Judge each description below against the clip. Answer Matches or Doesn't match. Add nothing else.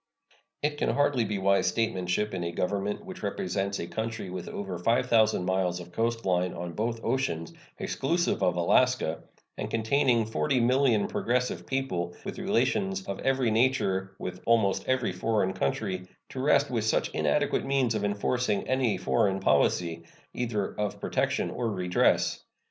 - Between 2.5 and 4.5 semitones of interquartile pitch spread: Doesn't match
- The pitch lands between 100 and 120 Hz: Matches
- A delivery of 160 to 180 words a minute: Doesn't match